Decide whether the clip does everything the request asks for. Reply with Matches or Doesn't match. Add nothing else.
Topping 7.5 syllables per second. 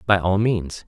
Doesn't match